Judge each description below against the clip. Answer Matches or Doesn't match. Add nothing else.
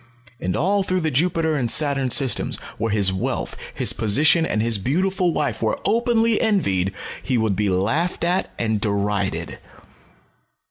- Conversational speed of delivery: Matches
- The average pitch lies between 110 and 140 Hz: Matches